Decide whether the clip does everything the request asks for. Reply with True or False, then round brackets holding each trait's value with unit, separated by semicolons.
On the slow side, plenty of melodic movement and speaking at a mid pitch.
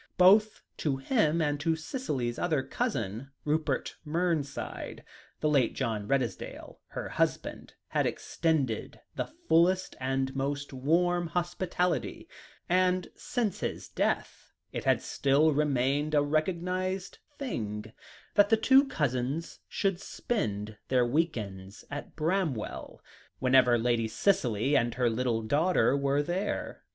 True (120 wpm; 5.9 semitones; 145 Hz)